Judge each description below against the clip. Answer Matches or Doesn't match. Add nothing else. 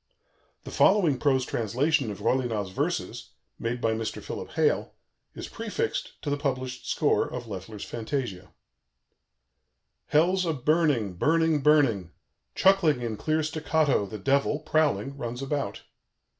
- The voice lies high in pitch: Doesn't match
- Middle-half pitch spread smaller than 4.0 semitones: Doesn't match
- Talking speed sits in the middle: Doesn't match